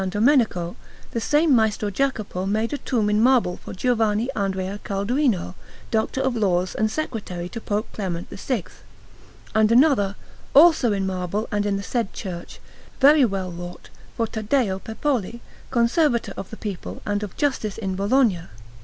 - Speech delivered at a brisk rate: No, average, 155 wpm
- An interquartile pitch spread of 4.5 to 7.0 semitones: No, average, 4.1 semitones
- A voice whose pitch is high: Yes, high, 215 Hz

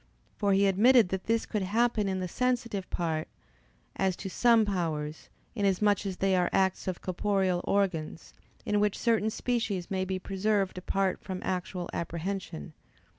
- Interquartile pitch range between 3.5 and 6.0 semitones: No, narrow, 2.4 semitones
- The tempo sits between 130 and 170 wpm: Yes, average, 155 wpm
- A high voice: Yes, high, 195 Hz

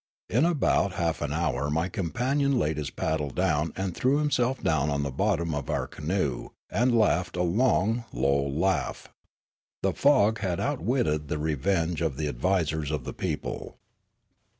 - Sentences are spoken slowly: No, average, 160 wpm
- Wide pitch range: Yes, wide, 6.8 semitones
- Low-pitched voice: Yes, very low, 85 Hz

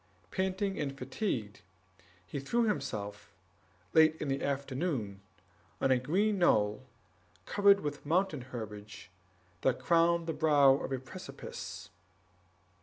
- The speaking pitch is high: No, medium, 140 Hz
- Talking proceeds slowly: Yes, slow, 115 wpm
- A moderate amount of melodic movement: No, wide, 5.7 semitones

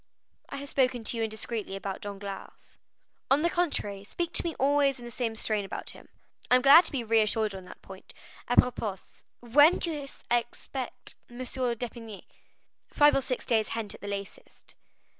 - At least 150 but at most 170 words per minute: No, average, 180 wpm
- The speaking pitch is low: No, high, 240 Hz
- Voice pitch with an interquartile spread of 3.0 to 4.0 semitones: No, average, 4.6 semitones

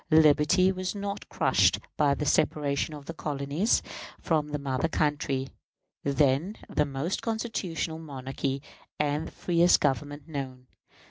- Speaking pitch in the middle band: Yes, medium, 150 Hz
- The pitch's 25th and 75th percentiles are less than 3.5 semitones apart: Yes, average, 2.9 semitones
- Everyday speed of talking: No, slow, 130 wpm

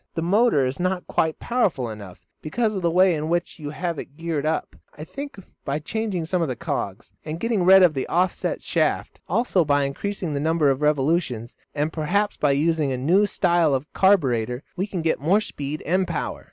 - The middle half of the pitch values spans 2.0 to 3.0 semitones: No, average, 4.5 semitones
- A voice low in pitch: No, medium, 160 Hz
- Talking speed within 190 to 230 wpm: Yes, fast, 205 wpm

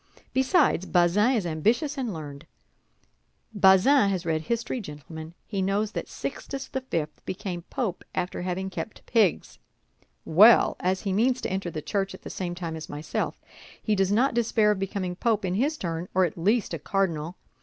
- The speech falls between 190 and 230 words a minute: No, average, 175 wpm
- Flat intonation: No, average, 4.5 semitones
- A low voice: No, high, 190 Hz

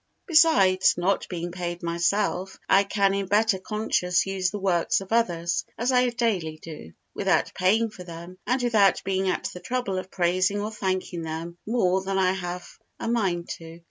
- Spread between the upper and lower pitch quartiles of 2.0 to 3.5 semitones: Yes, average, 2.9 semitones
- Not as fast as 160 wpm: No, average, 175 wpm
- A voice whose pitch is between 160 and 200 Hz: Yes, high, 190 Hz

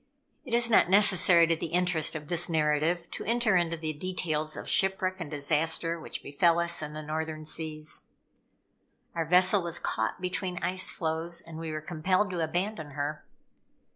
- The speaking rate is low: No, average, 170 wpm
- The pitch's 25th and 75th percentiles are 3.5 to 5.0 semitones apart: No, average, 2.7 semitones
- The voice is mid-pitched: Yes, medium, 165 Hz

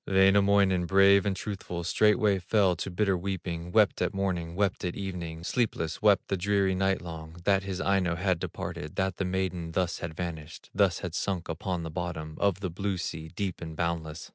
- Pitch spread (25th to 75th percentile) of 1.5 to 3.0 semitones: Yes, narrow, 2.5 semitones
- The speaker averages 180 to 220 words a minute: Yes, average, 190 wpm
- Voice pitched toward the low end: Yes, very low, 95 Hz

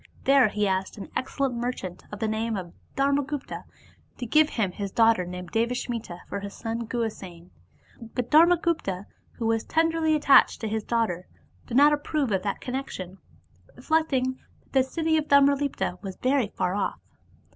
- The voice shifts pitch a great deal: Yes, wide, 5.9 semitones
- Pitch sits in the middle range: No, high, 235 Hz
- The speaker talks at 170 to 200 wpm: No, average, 160 wpm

